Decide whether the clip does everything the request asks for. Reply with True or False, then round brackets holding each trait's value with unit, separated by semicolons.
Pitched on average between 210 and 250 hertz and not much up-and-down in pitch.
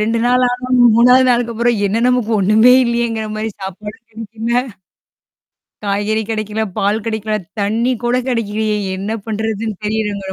True (220 Hz; 2.1 semitones)